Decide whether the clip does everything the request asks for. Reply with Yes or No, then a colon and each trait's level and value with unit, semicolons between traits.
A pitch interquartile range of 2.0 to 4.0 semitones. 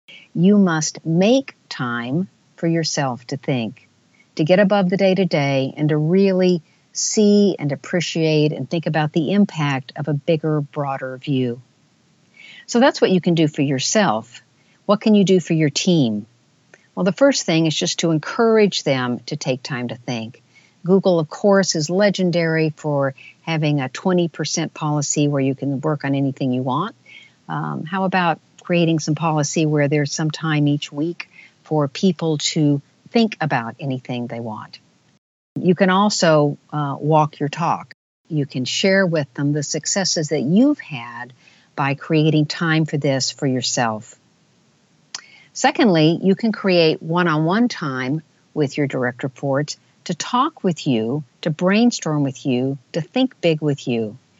No: average, 4.6 semitones